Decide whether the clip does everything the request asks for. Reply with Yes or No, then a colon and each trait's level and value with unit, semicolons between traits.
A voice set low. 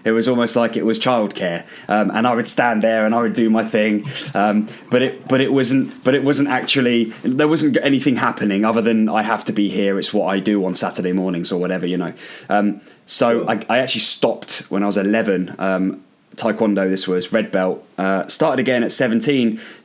Yes: low, 110 Hz